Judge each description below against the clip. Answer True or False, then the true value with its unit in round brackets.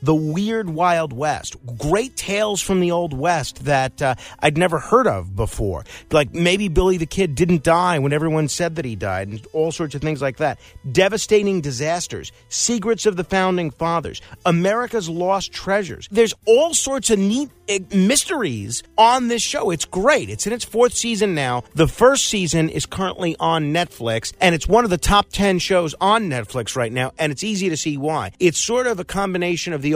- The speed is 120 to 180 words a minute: False (190 wpm)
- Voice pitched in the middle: True (175 Hz)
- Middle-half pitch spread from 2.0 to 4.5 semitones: False (5.2 semitones)